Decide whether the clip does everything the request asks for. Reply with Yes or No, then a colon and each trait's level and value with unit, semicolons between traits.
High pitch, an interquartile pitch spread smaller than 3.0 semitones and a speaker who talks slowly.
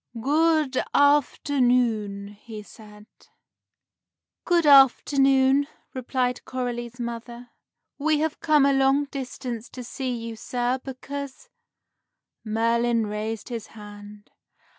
No: very high, 250 Hz; average, 3.5 semitones; slow, 100 wpm